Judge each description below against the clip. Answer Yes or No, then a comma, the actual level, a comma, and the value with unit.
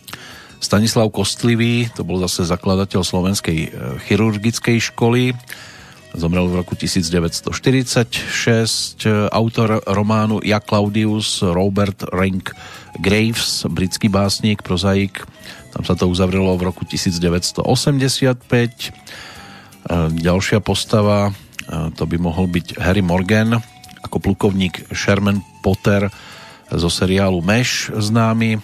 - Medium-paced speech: No, slow, 95 wpm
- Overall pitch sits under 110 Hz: Yes, low, 100 Hz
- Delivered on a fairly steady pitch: No, average, 3.3 semitones